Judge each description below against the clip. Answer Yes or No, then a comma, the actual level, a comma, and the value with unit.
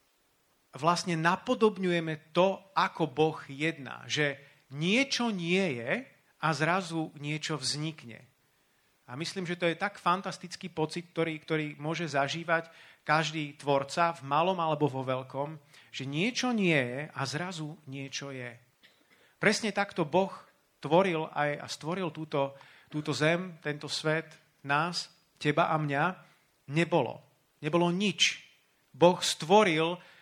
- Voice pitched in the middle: Yes, medium, 160 Hz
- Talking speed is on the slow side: No, average, 125 wpm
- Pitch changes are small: No, average, 3.0 semitones